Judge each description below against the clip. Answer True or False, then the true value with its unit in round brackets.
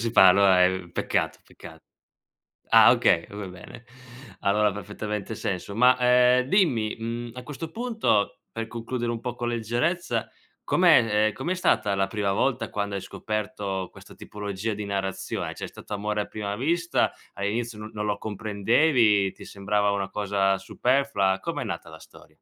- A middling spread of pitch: True (3.4 semitones)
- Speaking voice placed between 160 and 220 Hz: False (105 Hz)